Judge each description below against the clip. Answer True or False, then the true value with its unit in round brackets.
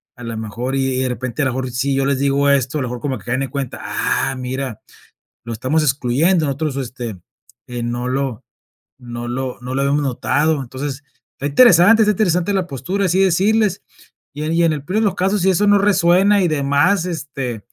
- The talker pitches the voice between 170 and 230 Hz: False (140 Hz)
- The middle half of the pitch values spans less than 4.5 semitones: False (5.3 semitones)